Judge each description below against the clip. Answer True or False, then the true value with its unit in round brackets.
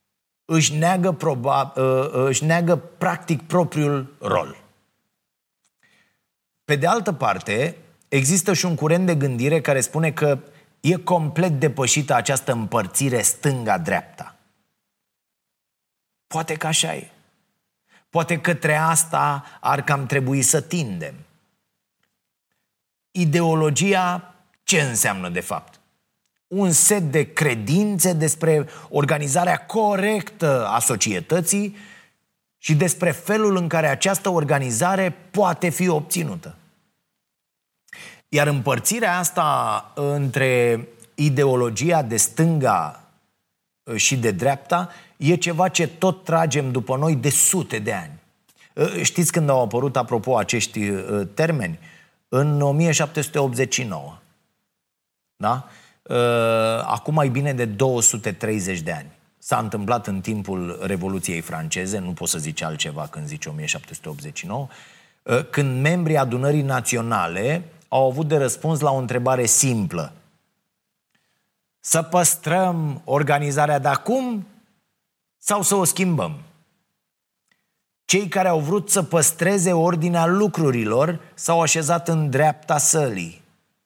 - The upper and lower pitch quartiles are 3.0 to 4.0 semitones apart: False (4.8 semitones)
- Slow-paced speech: True (105 wpm)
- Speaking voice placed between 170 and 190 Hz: False (155 Hz)